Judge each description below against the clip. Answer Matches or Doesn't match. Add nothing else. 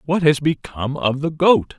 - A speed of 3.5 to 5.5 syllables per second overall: Matches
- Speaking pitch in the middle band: Matches